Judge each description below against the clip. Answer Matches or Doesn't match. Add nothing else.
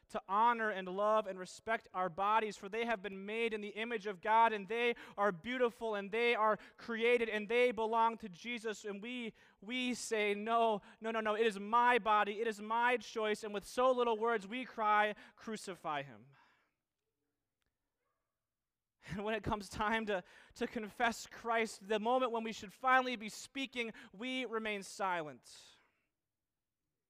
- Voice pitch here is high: Matches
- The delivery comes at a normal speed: Matches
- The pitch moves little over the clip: Matches